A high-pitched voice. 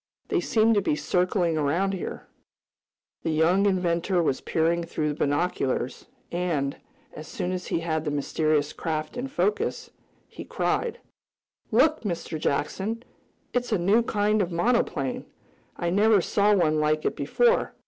No: medium, 175 Hz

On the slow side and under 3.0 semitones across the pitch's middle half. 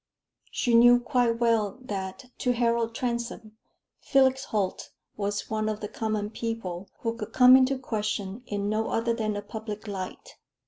No: average, 155 wpm; narrow, 2.6 semitones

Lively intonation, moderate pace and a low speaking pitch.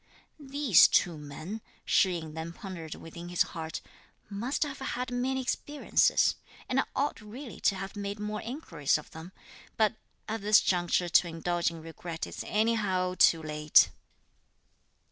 No: wide, 5.7 semitones; average, 150 wpm; high, 190 Hz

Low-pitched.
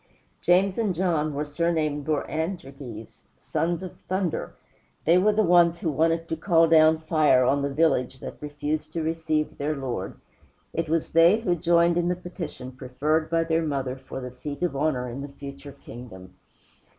No: medium, 155 Hz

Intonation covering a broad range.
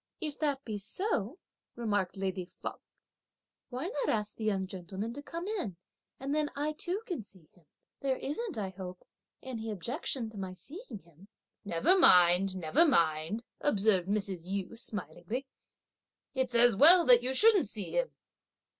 Yes: wide, 7.3 semitones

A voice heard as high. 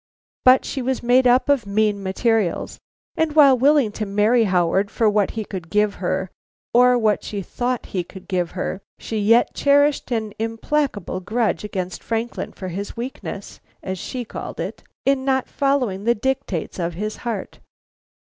Yes: high, 220 Hz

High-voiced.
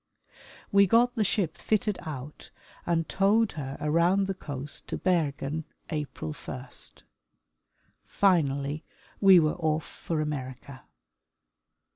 No: medium, 160 Hz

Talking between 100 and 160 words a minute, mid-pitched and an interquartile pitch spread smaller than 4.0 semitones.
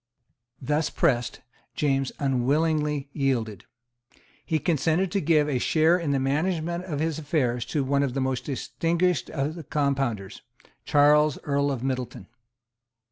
Yes: slow, 135 wpm; medium, 145 Hz; average, 2.9 semitones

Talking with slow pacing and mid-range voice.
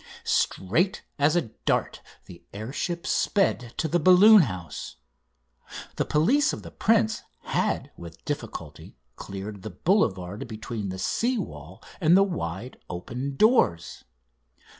No: slow, 130 wpm; low, 125 Hz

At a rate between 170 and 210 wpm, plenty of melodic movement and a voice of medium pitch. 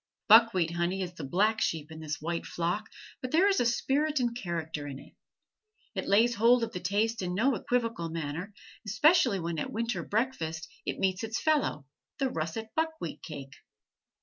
No: average, 175 wpm; wide, 6.1 semitones; high, 205 Hz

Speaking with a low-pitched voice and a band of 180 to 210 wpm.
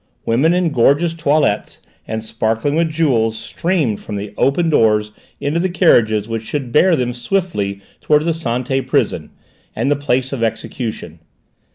No: low, 130 Hz; average, 155 wpm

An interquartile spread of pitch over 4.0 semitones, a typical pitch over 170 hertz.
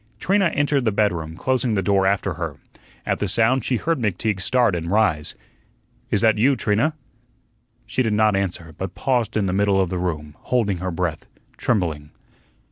No: average, 4.7 semitones; low, 100 Hz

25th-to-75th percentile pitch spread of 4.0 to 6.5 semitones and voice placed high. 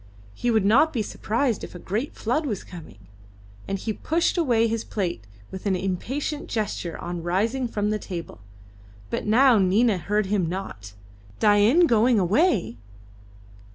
Yes: average, 4.5 semitones; high, 210 Hz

